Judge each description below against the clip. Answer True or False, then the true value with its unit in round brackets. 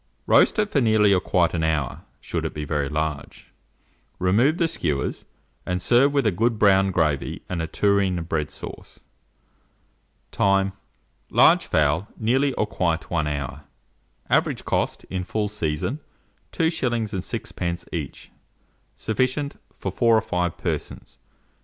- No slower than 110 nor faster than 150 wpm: True (140 wpm)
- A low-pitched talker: True (95 Hz)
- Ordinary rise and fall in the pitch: False (5.8 semitones)